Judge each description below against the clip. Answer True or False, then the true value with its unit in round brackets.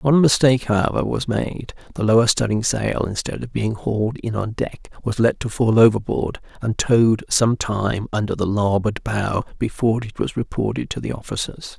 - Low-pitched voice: True (110 Hz)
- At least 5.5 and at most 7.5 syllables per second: False (5.1 syllables/s)